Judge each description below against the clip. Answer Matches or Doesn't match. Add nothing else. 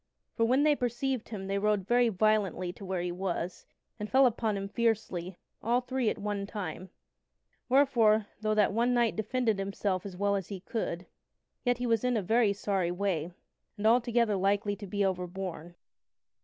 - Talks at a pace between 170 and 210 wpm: Matches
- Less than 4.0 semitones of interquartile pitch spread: Matches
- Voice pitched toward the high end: Matches